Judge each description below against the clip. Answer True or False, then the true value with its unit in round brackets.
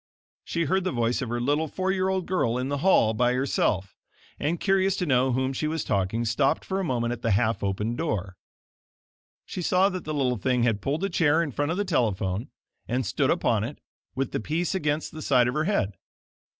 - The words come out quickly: True (225 wpm)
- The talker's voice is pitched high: False (135 Hz)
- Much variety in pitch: True (6.1 semitones)